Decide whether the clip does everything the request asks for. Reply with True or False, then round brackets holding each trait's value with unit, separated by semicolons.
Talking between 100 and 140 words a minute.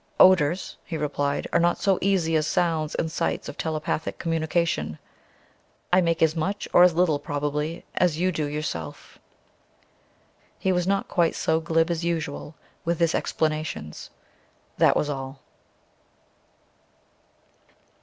True (135 wpm)